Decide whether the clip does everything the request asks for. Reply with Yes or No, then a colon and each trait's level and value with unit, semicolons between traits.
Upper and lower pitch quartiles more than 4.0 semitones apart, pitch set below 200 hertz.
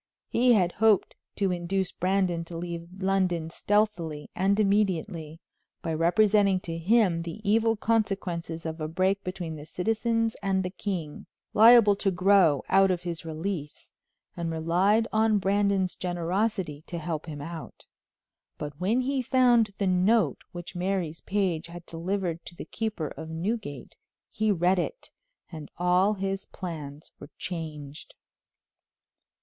No: average, 3.6 semitones; medium, 185 Hz